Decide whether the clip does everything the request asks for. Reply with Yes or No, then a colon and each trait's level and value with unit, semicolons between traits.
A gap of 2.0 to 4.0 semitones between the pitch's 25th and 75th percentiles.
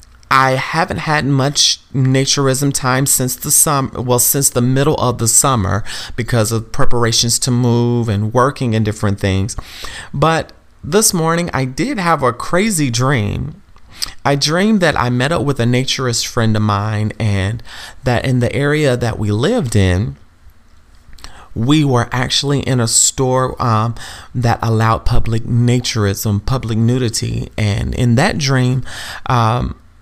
Yes: average, 3.6 semitones